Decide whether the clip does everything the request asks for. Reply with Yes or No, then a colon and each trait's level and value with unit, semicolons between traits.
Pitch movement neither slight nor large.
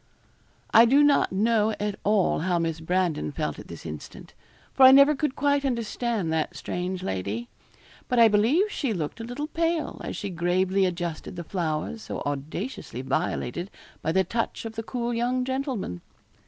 No: wide, 6.7 semitones